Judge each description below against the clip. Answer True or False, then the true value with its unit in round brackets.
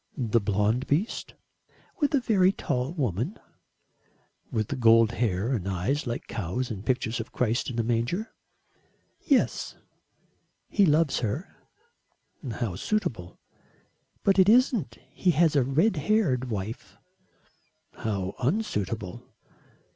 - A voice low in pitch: True (125 Hz)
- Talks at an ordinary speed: False (115 wpm)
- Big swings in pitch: True (7.7 semitones)